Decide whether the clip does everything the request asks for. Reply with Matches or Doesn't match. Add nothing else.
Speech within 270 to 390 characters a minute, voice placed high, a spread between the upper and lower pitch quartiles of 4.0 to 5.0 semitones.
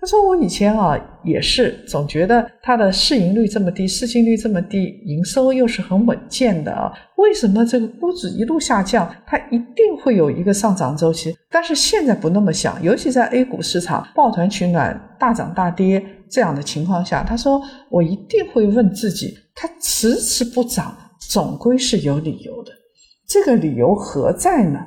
Doesn't match